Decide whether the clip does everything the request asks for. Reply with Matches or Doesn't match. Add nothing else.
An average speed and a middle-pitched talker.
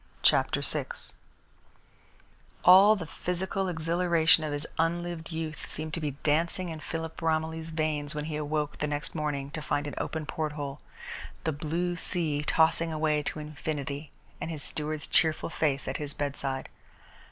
Matches